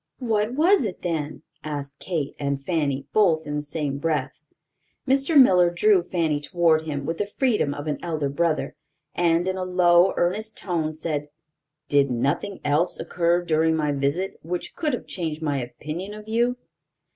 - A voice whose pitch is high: No, medium, 165 Hz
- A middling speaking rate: Yes, average, 170 wpm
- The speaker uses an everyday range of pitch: Yes, average, 4.2 semitones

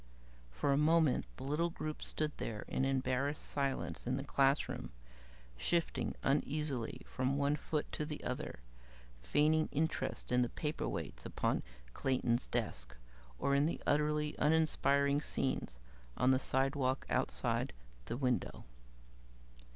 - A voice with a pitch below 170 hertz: Yes, medium, 140 Hz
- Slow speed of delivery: Yes, slow, 130 wpm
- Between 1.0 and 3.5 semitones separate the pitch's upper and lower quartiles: Yes, average, 2.9 semitones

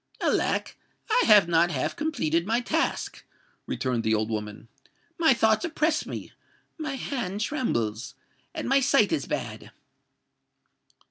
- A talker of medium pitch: No, high, 215 Hz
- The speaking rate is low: Yes, slow, 120 wpm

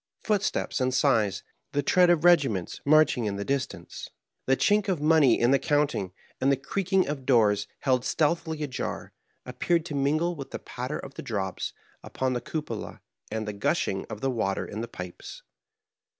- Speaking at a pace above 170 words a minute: Yes, average, 180 wpm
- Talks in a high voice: No, low, 135 Hz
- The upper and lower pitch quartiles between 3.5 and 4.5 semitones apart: No, average, 5.3 semitones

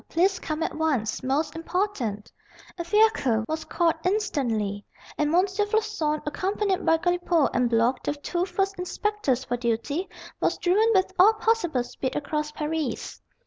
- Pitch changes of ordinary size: No, wide, 6.2 semitones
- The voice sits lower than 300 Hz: No, very high, 325 Hz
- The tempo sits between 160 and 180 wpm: No, average, 145 wpm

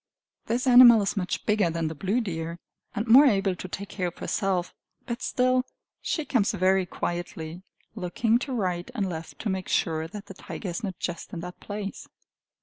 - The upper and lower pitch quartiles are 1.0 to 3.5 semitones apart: No, average, 4.3 semitones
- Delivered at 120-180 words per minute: No, average, 190 wpm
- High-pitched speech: Yes, high, 195 Hz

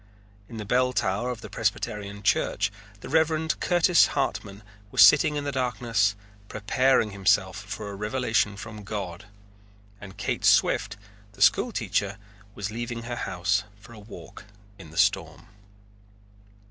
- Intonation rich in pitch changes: No, average, 3.8 semitones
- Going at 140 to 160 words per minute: Yes, average, 145 wpm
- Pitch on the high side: No, low, 105 Hz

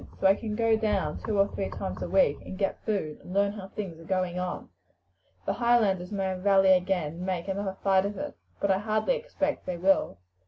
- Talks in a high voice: Yes, high, 195 Hz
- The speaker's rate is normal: No, fast, 220 wpm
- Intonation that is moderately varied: No, narrow, 2.1 semitones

